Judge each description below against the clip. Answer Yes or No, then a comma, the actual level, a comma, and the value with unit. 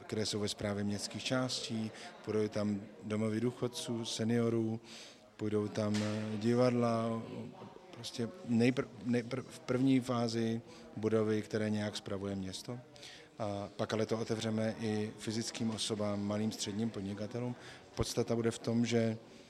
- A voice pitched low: Yes, low, 115 Hz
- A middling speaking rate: Yes, average, 125 wpm